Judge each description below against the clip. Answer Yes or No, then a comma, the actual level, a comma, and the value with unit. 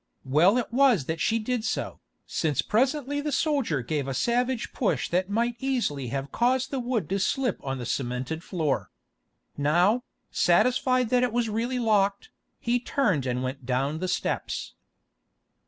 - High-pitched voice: Yes, high, 215 Hz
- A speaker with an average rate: Yes, average, 160 wpm